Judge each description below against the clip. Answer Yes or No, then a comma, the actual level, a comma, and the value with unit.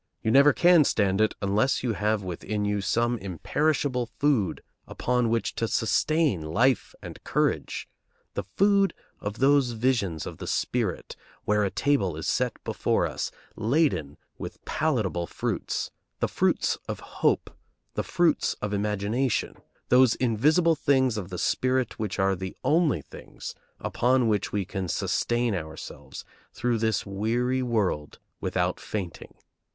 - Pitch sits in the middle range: No, low, 110 Hz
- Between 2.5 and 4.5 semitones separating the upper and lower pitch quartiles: No, average, 4.9 semitones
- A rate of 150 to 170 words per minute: No, average, 140 wpm